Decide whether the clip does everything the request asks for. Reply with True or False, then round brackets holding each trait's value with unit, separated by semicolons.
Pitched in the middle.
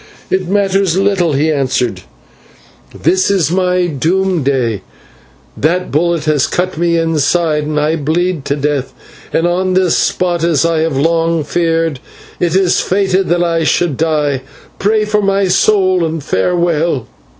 True (170 Hz)